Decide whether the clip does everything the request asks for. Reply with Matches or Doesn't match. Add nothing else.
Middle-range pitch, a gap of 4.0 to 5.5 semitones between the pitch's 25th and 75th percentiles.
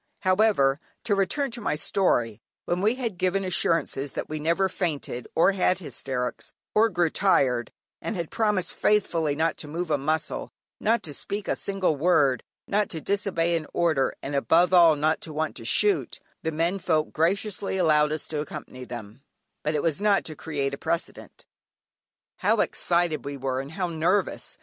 Matches